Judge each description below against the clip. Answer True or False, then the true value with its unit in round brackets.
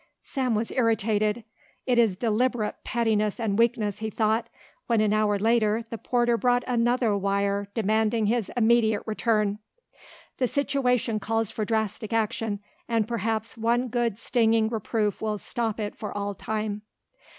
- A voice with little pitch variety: True (1.9 semitones)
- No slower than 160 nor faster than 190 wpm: False (145 wpm)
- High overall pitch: True (220 Hz)